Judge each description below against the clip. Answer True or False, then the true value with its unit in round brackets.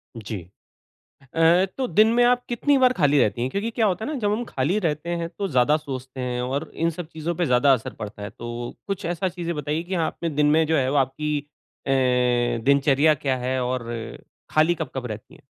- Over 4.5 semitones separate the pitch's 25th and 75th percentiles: True (5.3 semitones)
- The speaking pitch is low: False (155 Hz)